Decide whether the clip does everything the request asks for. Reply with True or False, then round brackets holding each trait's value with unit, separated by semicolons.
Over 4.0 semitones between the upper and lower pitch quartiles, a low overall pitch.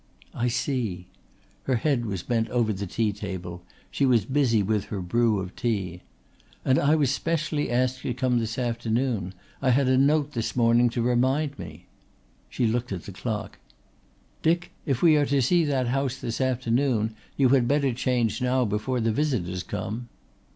False (3.6 semitones; 120 Hz)